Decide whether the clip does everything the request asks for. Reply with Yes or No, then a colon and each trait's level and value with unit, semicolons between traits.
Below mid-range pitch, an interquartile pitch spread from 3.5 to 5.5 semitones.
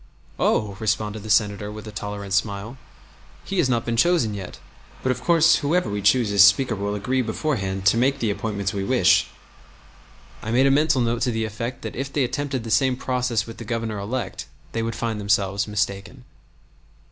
Yes: low, 110 Hz; average, 3.9 semitones